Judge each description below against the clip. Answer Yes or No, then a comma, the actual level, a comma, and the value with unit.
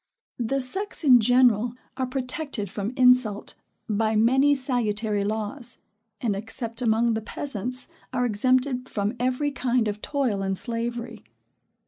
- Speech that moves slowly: Yes, slow, 130 wpm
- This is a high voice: Yes, high, 240 Hz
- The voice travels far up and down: No, average, 2.9 semitones